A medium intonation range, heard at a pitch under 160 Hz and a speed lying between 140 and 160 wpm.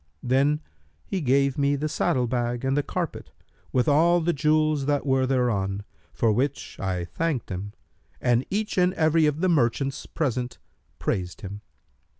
Yes: average, 4.3 semitones; low, 135 Hz; average, 155 wpm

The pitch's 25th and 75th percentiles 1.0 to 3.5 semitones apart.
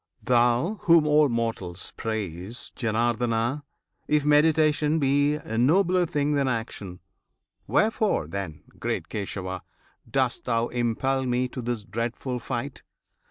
No: average, 4.7 semitones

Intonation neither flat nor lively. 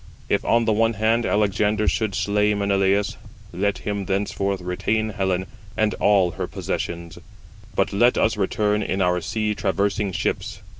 No: narrow, 1.8 semitones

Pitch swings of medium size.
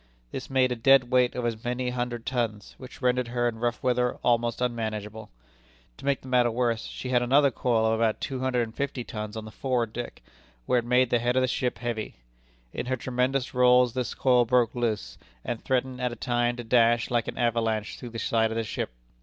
No: narrow, 1.7 semitones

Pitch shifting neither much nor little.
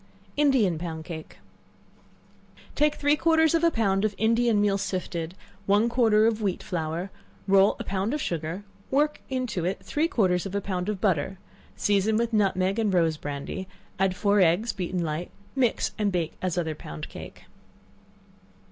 Yes: average, 4.3 semitones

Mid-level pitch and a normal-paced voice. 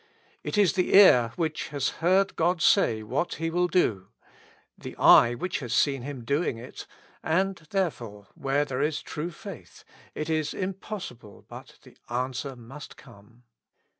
Yes: medium, 145 Hz; average, 160 wpm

